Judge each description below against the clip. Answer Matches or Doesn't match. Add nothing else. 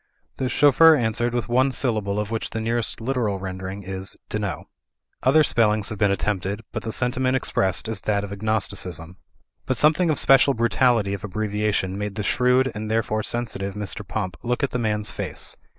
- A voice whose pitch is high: Doesn't match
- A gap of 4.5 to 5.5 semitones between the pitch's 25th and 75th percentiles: Doesn't match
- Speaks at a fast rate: Doesn't match